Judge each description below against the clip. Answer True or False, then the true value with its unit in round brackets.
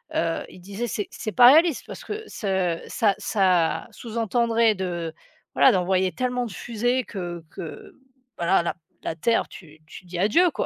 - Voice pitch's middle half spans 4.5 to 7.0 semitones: True (5.2 semitones)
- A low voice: False (195 Hz)